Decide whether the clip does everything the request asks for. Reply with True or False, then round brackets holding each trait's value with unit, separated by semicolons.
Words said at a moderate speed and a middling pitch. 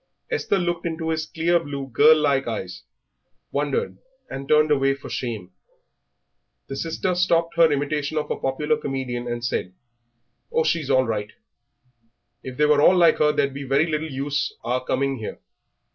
True (165 wpm; 145 Hz)